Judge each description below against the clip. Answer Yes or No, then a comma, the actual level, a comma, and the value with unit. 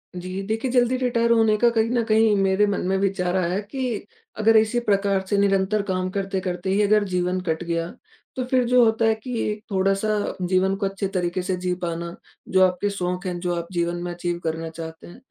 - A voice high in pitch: Yes, high, 195 Hz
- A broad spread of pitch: No, average, 3.3 semitones